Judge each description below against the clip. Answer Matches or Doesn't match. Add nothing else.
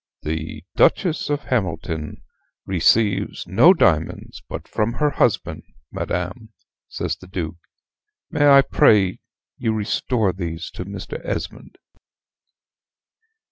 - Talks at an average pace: Doesn't match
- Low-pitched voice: Matches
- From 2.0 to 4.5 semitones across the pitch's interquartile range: Doesn't match